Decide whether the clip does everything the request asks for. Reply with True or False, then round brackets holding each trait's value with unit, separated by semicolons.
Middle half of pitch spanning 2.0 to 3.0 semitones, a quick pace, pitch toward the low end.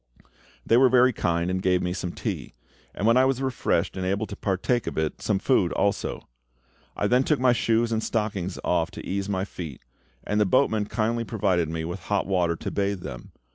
False (4.3 semitones; 210 wpm; 100 Hz)